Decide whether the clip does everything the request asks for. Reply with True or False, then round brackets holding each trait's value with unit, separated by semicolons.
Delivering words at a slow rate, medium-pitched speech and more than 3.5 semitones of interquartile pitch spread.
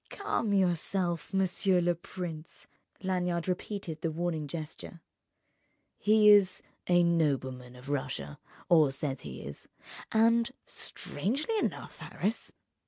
True (105 wpm; 175 Hz; 4.2 semitones)